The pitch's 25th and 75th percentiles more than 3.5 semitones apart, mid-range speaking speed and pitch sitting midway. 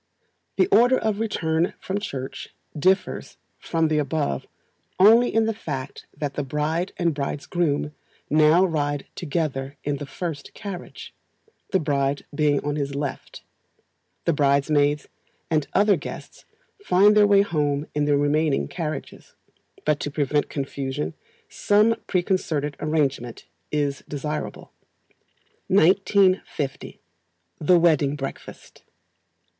No: average, 4.2 semitones; slow, 120 wpm; medium, 150 Hz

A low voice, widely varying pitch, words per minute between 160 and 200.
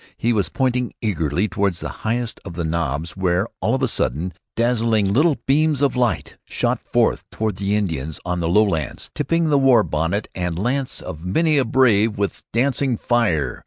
Yes: low, 105 Hz; wide, 6.2 semitones; average, 180 wpm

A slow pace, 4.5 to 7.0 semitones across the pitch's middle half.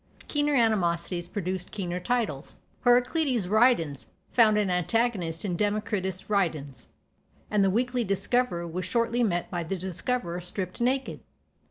Yes: slow, 130 wpm; average, 5.3 semitones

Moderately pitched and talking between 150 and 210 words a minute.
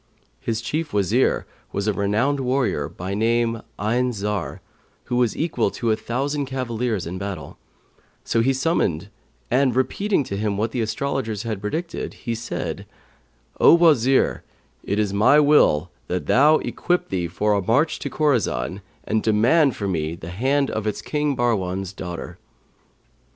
No: low, 115 Hz; average, 155 wpm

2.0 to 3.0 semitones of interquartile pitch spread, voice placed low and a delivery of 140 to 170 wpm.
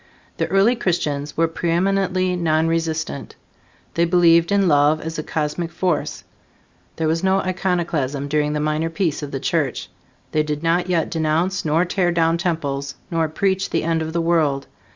No: narrow, 2.5 semitones; medium, 165 Hz; average, 165 wpm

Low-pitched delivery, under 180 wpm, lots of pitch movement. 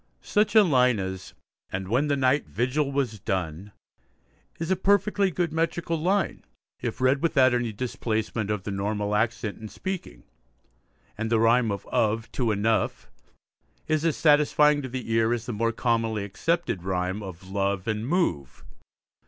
Yes: low, 115 Hz; average, 160 wpm; wide, 6.4 semitones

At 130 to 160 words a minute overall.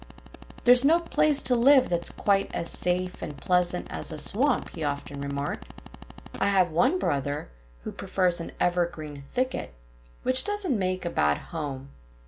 Yes: average, 155 wpm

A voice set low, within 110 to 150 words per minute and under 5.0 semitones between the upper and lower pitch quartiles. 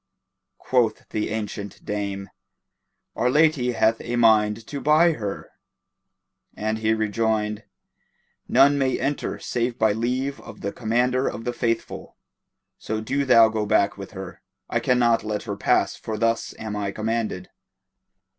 Yes: low, 110 Hz; average, 145 wpm; narrow, 2.6 semitones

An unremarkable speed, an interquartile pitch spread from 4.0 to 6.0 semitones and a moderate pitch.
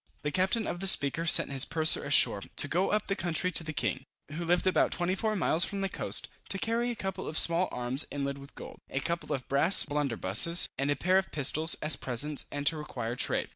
No: fast, 225 wpm; average, 4.9 semitones; medium, 160 Hz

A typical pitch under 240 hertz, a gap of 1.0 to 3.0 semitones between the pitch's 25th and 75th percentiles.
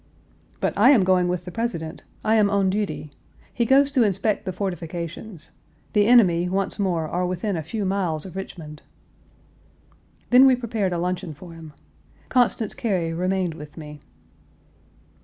No: medium, 185 Hz; average, 4.0 semitones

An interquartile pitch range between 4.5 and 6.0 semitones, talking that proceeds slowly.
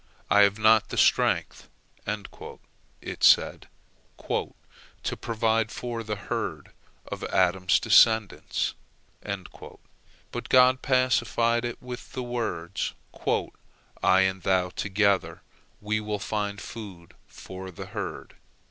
No: average, 3.3 semitones; slow, 110 wpm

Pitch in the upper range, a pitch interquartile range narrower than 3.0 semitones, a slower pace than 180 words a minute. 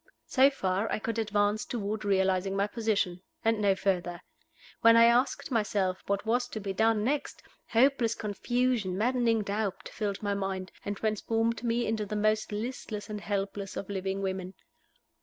Yes: high, 210 Hz; narrow, 2.6 semitones; average, 160 wpm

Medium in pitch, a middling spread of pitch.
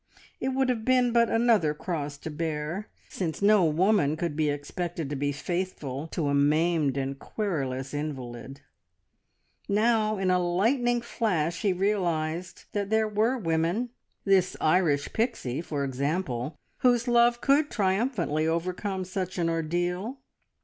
No: medium, 175 Hz; wide, 6.1 semitones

